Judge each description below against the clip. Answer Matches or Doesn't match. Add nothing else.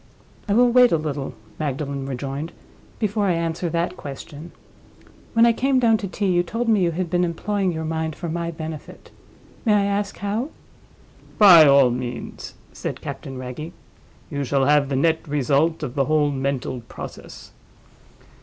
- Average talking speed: Matches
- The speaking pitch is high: Doesn't match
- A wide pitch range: Matches